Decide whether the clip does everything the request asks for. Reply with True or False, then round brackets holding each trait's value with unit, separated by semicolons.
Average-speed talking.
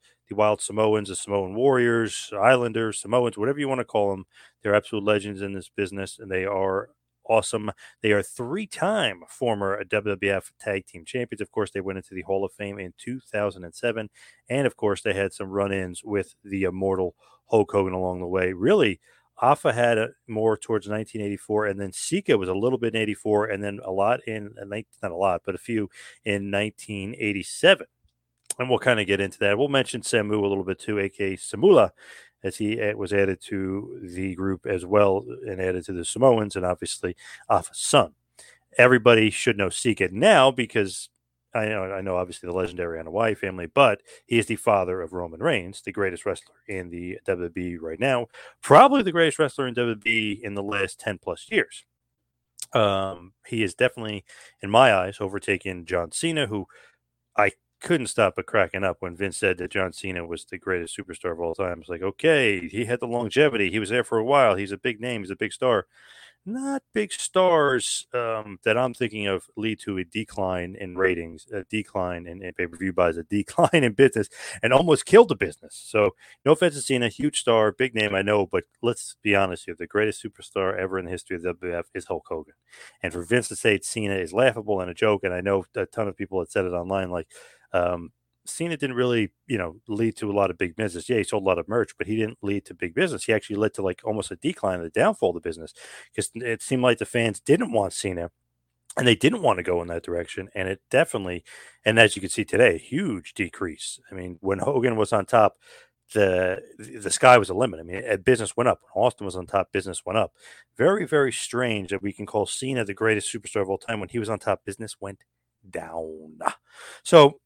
False (215 wpm)